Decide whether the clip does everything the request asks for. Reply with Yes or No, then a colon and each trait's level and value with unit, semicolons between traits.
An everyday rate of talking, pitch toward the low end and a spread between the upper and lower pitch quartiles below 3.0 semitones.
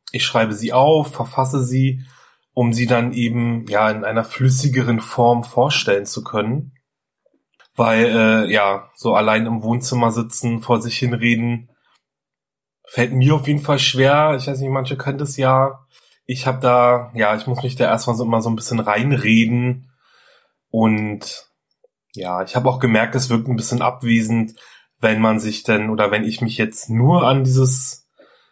Yes: average, 170 wpm; low, 120 Hz; narrow, 2.6 semitones